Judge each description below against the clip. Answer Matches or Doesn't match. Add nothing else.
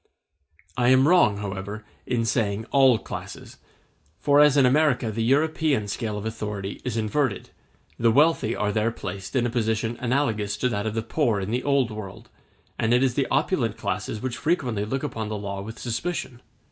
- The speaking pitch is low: Matches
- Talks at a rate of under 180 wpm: Doesn't match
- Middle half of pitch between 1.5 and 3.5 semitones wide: Doesn't match